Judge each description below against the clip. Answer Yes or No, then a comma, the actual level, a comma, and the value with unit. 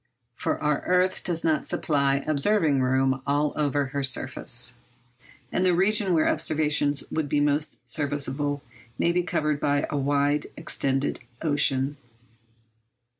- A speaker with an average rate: No, slow, 130 wpm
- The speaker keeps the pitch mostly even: Yes, narrow, 2.2 semitones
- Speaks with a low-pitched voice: No, medium, 145 Hz